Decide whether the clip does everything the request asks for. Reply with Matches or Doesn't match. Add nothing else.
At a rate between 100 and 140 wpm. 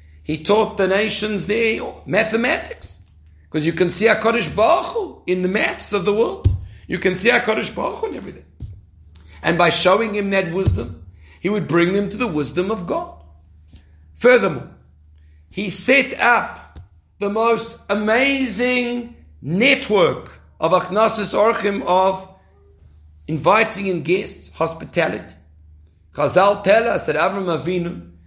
Matches